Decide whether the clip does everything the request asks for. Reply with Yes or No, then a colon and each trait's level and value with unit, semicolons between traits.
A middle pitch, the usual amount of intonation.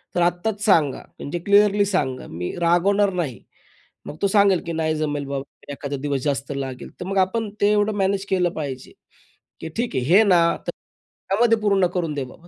No: medium, 175 Hz; wide, 5.7 semitones